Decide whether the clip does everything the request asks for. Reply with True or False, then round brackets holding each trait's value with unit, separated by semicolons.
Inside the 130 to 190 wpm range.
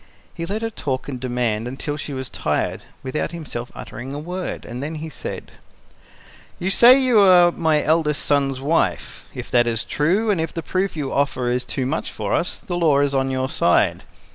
False (200 wpm)